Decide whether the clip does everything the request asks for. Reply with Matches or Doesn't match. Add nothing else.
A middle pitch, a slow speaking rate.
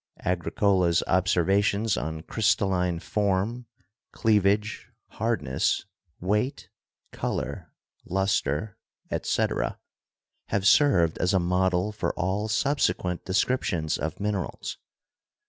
Doesn't match